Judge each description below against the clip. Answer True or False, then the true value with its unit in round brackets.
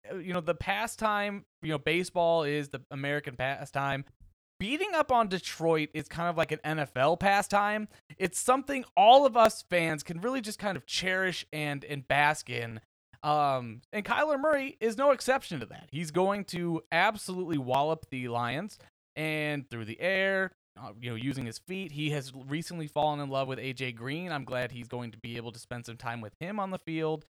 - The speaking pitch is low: False (155 Hz)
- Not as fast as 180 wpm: False (195 wpm)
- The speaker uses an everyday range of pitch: False (5.8 semitones)